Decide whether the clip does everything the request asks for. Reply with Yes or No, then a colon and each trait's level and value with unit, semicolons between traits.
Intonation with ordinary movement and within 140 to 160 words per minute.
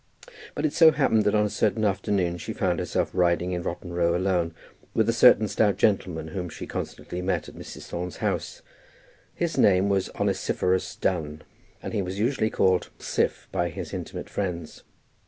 No: average, 3.2 semitones; average, 175 wpm